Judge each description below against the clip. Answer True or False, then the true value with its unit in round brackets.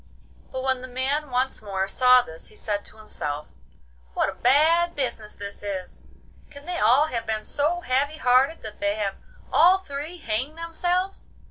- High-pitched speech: True (255 Hz)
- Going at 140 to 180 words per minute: True (170 wpm)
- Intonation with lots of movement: True (6.3 semitones)